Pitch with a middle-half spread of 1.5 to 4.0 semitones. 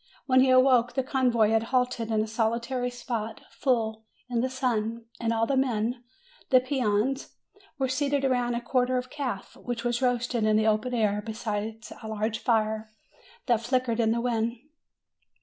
Yes: narrow, 2.4 semitones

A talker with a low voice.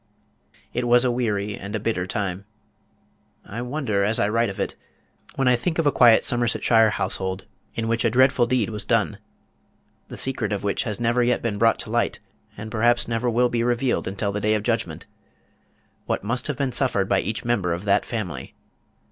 Yes: low, 115 Hz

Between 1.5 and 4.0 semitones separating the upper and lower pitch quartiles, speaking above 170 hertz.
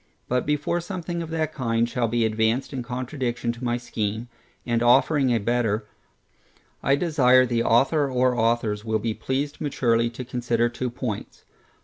No: narrow, 2.6 semitones; low, 120 Hz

